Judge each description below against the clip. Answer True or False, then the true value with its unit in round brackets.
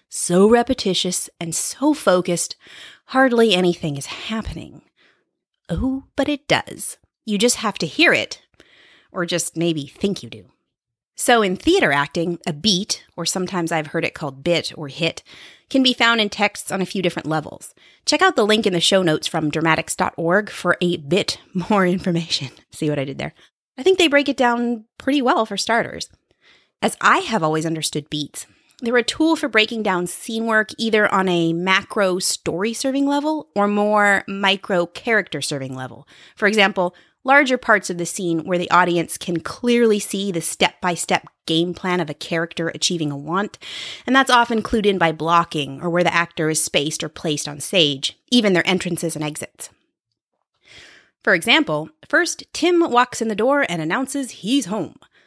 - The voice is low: False (185 Hz)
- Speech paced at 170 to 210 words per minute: True (180 wpm)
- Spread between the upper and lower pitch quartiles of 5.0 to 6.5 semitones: True (5.5 semitones)